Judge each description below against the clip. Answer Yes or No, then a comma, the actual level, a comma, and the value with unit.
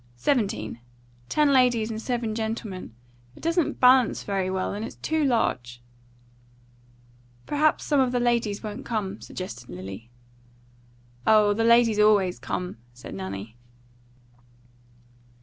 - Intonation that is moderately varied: Yes, average, 4.8 semitones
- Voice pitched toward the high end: Yes, high, 215 Hz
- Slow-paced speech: Yes, slow, 120 wpm